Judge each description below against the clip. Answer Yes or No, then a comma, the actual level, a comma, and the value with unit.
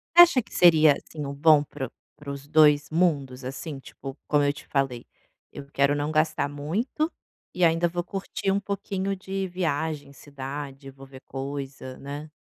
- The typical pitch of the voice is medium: Yes, medium, 145 Hz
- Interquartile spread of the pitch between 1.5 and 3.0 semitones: No, average, 3.8 semitones